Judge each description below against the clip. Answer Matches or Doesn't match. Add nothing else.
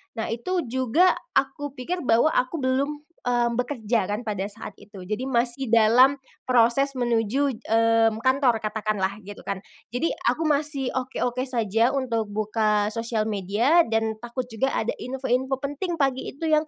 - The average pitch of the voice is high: Matches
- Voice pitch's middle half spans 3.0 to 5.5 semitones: Matches